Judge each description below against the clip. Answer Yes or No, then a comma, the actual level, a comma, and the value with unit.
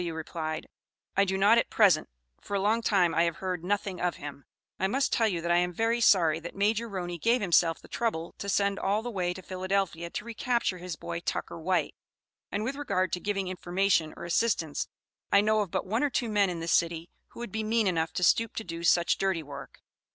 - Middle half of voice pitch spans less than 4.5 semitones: Yes, average, 3.8 semitones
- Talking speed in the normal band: No, fast, 230 wpm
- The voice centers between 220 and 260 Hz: No, medium, 185 Hz